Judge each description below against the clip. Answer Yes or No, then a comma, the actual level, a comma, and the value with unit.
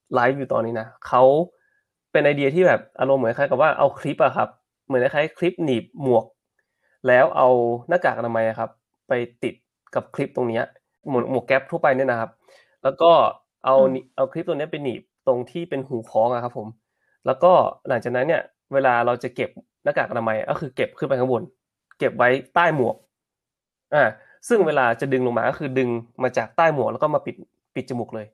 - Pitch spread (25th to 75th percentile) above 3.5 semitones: No, average, 3.0 semitones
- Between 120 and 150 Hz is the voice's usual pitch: Yes, low, 130 Hz